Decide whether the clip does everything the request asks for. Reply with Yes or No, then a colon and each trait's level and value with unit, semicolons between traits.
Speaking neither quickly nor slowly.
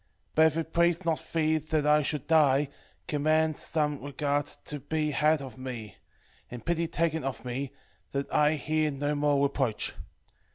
Yes: average, 165 wpm